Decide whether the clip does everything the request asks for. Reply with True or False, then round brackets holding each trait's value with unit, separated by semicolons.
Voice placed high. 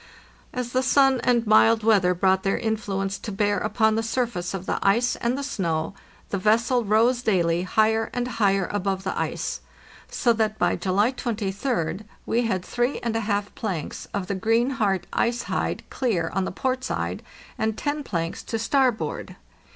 True (220 Hz)